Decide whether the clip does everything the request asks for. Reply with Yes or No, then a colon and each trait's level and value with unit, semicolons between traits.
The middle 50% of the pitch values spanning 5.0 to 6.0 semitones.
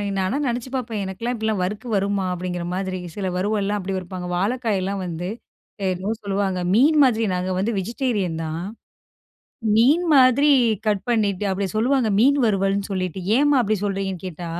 No: average, 3.8 semitones